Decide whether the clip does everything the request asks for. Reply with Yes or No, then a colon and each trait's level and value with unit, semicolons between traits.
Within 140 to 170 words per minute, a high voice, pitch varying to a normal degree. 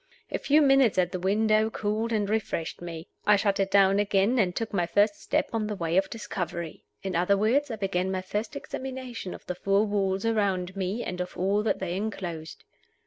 No: fast, 205 wpm; high, 200 Hz; average, 3.1 semitones